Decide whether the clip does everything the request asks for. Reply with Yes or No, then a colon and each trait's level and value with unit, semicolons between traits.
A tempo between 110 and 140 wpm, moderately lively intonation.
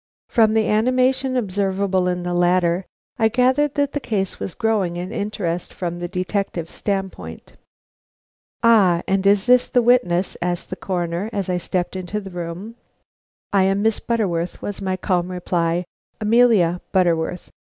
No: average, 155 wpm; average, 3.8 semitones